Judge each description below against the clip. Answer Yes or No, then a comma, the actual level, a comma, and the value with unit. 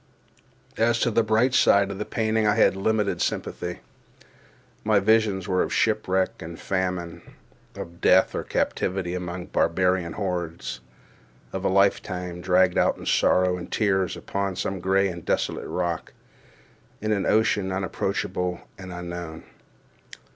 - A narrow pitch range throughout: Yes, narrow, 2.1 semitones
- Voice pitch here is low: Yes, very low, 95 Hz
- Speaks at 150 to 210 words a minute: No, average, 140 wpm